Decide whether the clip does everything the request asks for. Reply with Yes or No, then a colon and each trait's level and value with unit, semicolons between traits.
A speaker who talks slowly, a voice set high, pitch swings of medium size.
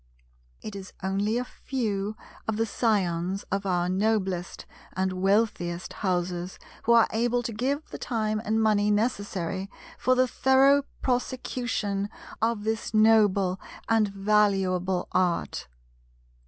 Yes: slow, 125 wpm; high, 210 Hz; average, 3.1 semitones